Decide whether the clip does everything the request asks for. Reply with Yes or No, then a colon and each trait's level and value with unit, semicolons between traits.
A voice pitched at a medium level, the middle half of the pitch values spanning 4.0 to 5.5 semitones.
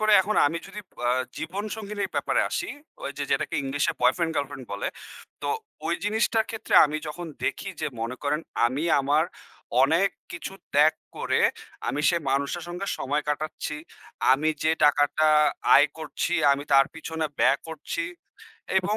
Yes: medium, 155 Hz; average, 4.3 semitones